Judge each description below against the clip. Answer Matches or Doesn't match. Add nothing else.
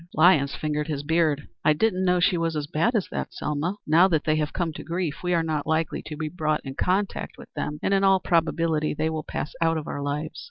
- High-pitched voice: Doesn't match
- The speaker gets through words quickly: Matches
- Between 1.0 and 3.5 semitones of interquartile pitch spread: Matches